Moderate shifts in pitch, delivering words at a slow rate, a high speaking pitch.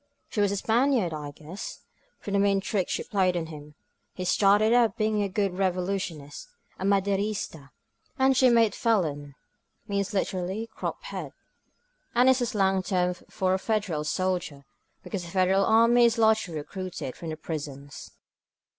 No: average, 3.9 semitones; average, 175 wpm; high, 195 Hz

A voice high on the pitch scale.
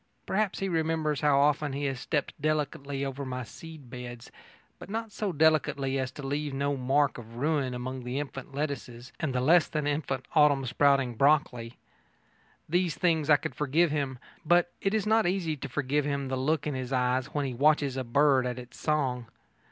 No: medium, 140 Hz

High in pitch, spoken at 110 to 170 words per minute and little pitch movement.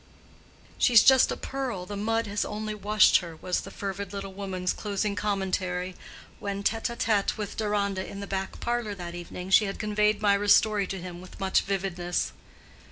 No: high, 200 Hz; average, 180 wpm; narrow, 2.0 semitones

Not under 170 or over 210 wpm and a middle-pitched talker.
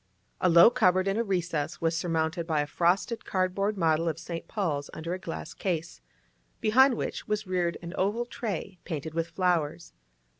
Yes: average, 175 wpm; medium, 175 Hz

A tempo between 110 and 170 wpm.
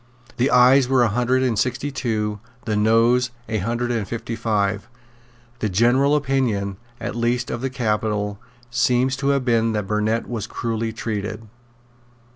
Yes: average, 155 wpm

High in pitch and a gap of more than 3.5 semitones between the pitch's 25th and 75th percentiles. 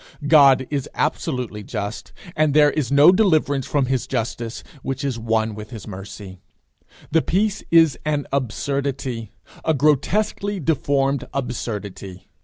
No: low, 135 Hz; average, 4.9 semitones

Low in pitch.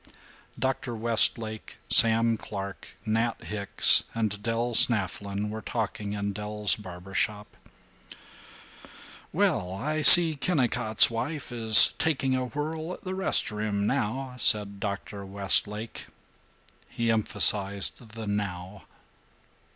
Yes: low, 110 Hz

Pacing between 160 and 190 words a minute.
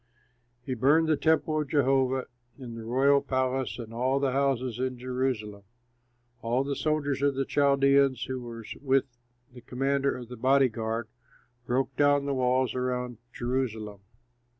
No: average, 150 wpm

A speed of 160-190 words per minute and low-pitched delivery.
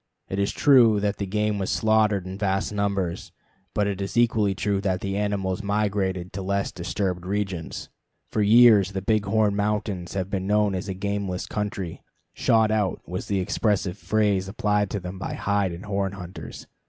Yes: average, 180 wpm; low, 100 Hz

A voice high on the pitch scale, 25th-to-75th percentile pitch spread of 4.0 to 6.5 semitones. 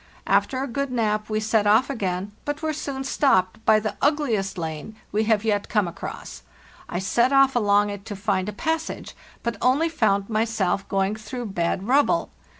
Yes: high, 215 Hz; average, 4.7 semitones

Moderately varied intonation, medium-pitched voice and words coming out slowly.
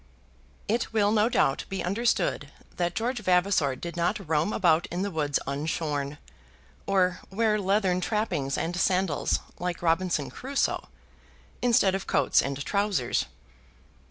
Yes: average, 4.2 semitones; medium, 180 Hz; slow, 130 wpm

